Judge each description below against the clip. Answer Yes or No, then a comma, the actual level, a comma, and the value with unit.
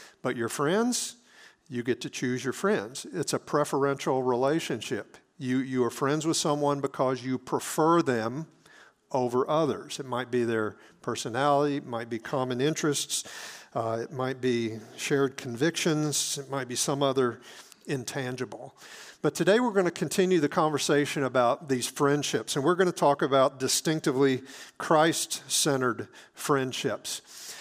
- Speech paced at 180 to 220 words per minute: No, average, 150 wpm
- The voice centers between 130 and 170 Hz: Yes, medium, 140 Hz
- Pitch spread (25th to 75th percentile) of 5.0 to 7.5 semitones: No, average, 3.1 semitones